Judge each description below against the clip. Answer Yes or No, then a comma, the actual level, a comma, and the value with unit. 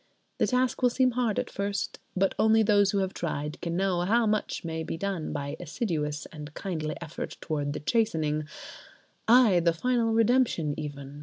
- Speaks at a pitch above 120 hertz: Yes, medium, 185 Hz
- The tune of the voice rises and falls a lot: Yes, wide, 6.4 semitones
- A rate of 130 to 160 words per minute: No, average, 170 wpm